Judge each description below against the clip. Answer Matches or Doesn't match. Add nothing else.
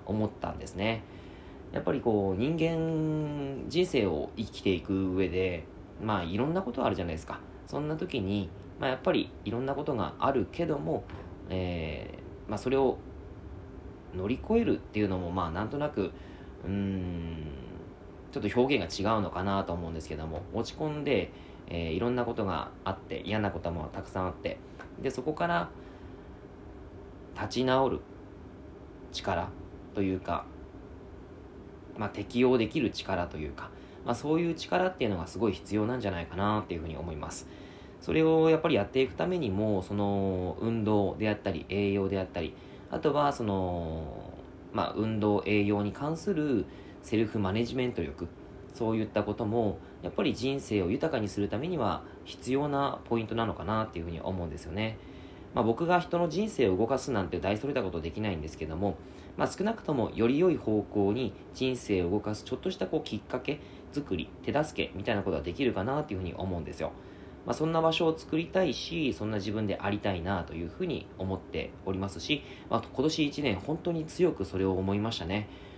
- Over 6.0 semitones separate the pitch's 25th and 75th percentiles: Doesn't match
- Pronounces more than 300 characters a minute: Matches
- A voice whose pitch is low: Matches